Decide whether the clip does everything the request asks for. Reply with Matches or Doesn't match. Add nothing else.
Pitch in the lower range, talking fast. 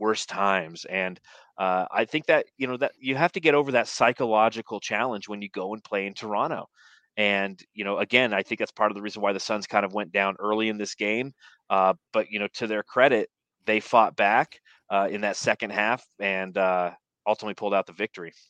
Matches